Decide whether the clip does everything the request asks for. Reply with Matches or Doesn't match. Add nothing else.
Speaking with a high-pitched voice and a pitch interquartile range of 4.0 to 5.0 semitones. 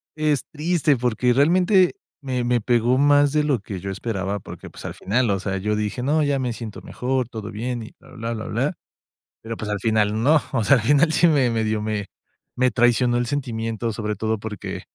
Doesn't match